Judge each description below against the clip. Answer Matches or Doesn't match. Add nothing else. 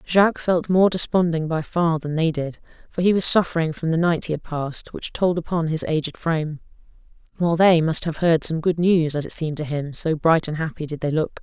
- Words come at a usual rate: Doesn't match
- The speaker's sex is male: Doesn't match